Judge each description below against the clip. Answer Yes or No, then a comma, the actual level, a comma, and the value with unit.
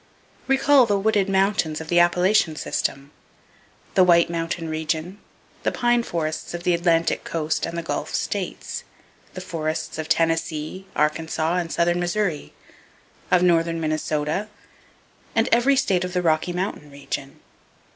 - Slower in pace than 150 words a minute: Yes, average, 140 wpm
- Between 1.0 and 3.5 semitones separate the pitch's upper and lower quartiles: Yes, average, 2.9 semitones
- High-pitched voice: No, medium, 170 Hz